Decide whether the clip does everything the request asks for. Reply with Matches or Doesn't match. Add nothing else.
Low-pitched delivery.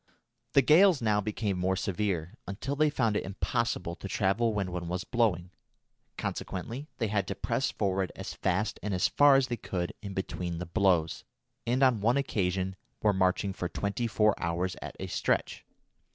Matches